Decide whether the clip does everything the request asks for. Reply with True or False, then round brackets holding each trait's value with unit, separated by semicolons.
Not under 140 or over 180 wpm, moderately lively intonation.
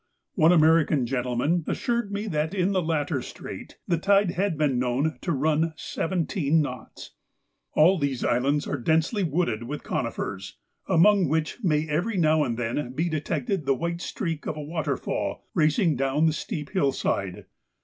True (160 wpm; 3.6 semitones)